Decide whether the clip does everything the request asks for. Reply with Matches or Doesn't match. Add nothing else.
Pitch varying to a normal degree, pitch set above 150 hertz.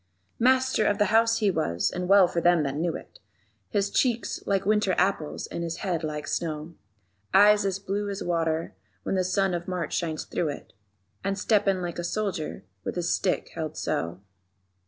Matches